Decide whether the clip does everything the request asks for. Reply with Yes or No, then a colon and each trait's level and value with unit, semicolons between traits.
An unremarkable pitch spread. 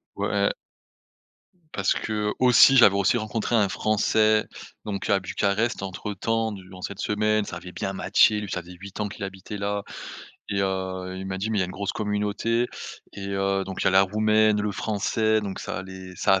No: narrow, 2.0 semitones